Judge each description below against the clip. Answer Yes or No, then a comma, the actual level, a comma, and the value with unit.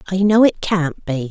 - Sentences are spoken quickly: Yes, fast, 230 wpm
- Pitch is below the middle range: No, medium, 180 Hz